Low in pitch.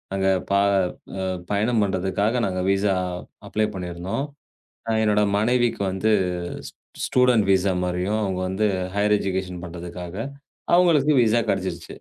Yes: low, 100 Hz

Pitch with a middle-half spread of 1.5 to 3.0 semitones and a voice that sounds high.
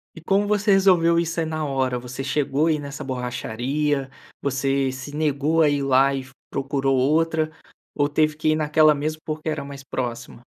No: average, 2.7 semitones; medium, 145 Hz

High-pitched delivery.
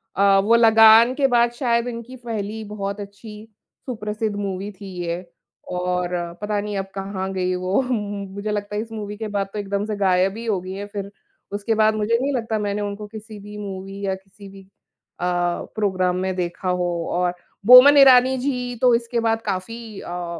Yes: high, 205 Hz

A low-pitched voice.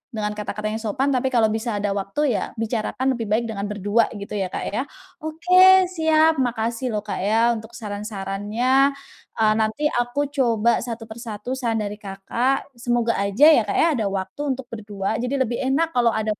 No: high, 230 Hz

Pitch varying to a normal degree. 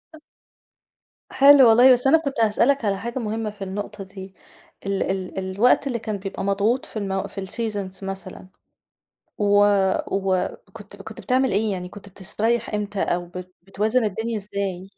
Yes: average, 3.0 semitones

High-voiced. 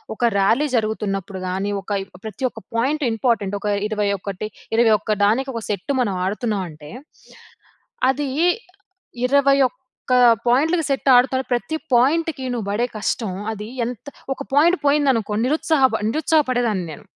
Yes: high, 235 Hz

